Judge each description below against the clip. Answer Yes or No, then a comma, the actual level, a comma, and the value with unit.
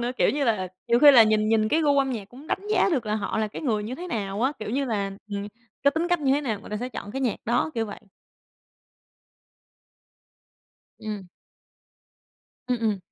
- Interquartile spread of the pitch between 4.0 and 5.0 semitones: Yes, average, 4.4 semitones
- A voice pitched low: No, high, 230 Hz